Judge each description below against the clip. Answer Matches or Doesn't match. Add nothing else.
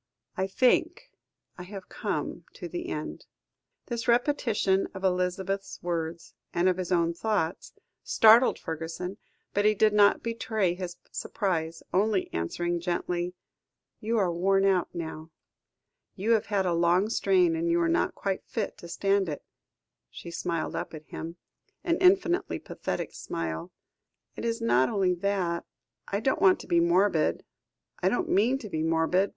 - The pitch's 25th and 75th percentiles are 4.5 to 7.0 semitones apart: Doesn't match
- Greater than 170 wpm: Doesn't match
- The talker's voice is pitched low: Doesn't match